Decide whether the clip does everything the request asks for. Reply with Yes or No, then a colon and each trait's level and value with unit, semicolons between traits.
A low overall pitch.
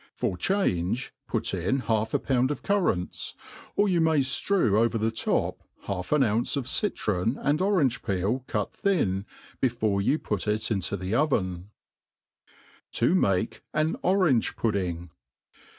Yes: low, 115 Hz